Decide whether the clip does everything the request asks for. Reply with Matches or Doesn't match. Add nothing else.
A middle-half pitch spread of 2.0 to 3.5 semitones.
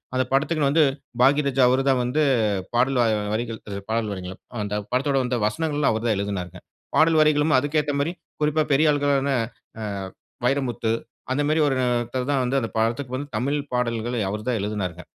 Doesn't match